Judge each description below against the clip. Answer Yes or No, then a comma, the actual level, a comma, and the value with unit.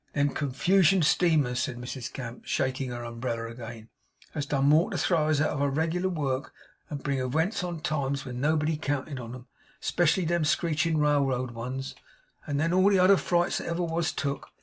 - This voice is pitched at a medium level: Yes, medium, 145 Hz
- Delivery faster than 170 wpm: Yes, average, 190 wpm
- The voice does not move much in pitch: No, average, 4.3 semitones